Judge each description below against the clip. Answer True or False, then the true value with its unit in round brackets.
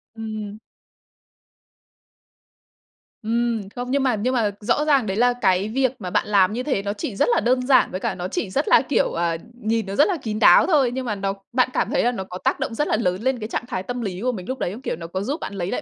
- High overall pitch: True (225 Hz)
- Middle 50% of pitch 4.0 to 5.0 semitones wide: True (4.4 semitones)